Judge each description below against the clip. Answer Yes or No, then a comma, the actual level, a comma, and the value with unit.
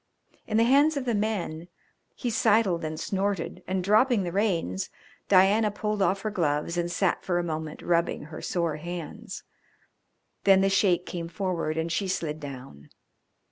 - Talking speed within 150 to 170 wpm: Yes, average, 165 wpm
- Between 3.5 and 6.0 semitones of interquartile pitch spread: Yes, average, 3.8 semitones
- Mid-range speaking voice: Yes, medium, 180 Hz